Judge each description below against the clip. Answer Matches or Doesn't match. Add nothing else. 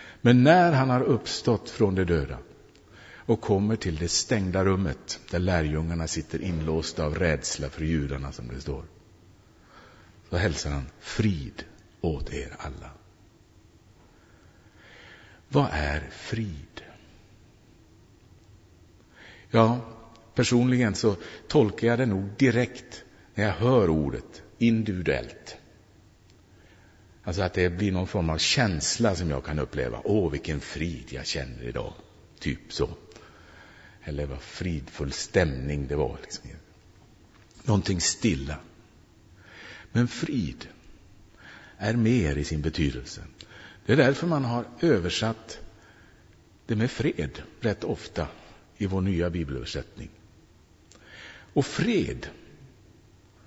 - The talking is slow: Matches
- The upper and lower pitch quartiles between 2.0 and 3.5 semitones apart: Doesn't match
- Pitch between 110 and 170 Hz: Doesn't match